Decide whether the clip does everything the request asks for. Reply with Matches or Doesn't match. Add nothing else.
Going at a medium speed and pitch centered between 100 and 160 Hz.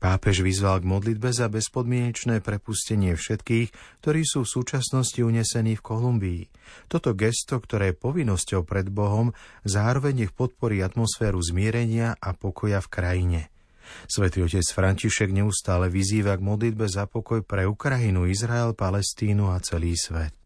Matches